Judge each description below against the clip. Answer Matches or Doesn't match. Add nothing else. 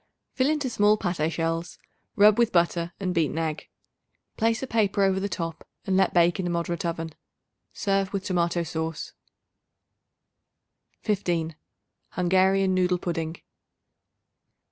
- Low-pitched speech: Doesn't match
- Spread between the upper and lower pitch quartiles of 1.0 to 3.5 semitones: Matches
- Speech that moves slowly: Matches